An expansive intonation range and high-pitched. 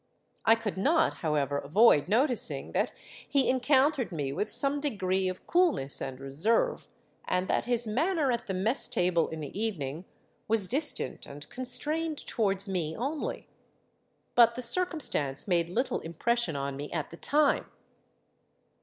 Yes: wide, 8.5 semitones; high, 215 Hz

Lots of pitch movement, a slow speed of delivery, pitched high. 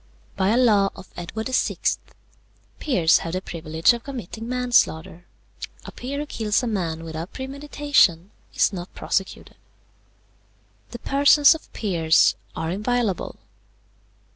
Yes: wide, 6.7 semitones; slow, 130 wpm; high, 210 Hz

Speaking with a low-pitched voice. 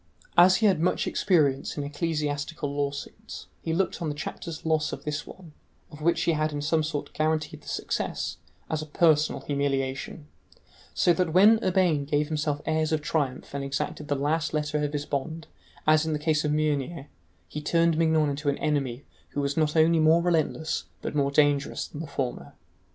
No: medium, 150 Hz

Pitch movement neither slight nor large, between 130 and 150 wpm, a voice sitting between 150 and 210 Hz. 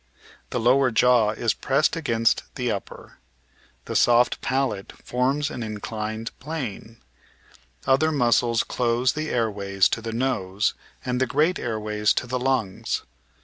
No: average, 3.2 semitones; average, 140 wpm; low, 120 Hz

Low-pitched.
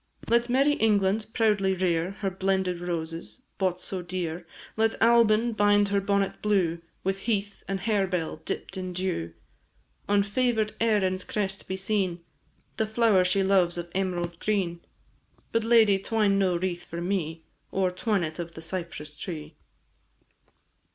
No: high, 190 Hz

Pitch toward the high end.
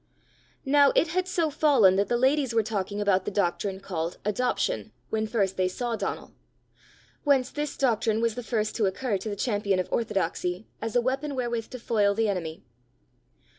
Yes: high, 220 Hz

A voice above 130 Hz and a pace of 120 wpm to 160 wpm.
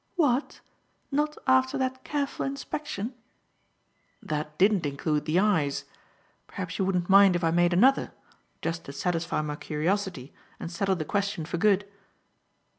Yes: medium, 185 Hz; average, 140 wpm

